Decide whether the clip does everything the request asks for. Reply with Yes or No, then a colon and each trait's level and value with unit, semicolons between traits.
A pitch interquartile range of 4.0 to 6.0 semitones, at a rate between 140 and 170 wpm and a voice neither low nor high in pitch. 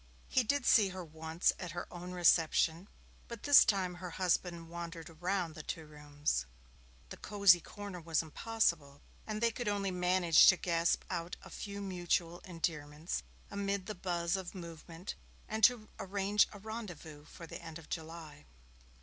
No: average, 3.4 semitones; average, 160 wpm; medium, 175 Hz